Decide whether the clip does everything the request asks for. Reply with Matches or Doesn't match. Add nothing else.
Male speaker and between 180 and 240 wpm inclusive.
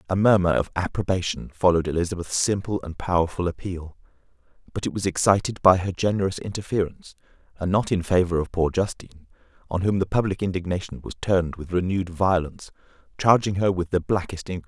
Doesn't match